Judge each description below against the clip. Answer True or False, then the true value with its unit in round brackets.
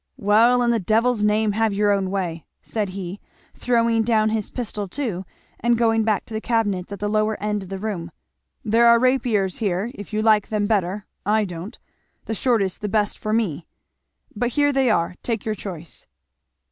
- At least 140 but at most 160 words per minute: False (190 wpm)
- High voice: True (215 Hz)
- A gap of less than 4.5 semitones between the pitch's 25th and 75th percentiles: True (2.5 semitones)